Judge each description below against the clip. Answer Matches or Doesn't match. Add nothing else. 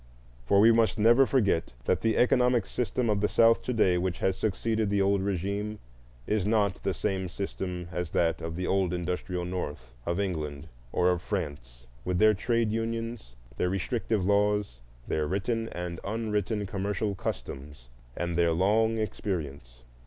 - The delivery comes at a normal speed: Matches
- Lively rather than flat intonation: Doesn't match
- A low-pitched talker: Matches